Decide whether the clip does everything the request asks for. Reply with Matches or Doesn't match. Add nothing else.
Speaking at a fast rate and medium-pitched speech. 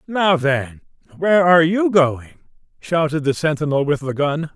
Doesn't match